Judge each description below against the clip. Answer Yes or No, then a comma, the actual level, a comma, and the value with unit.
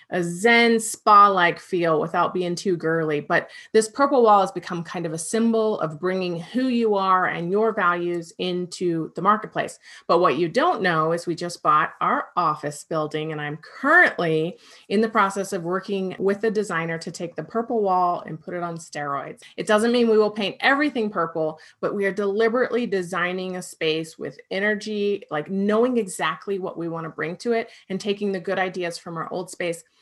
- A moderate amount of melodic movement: Yes, average, 4.1 semitones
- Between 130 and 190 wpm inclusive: No, average, 200 wpm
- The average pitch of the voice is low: No, medium, 185 Hz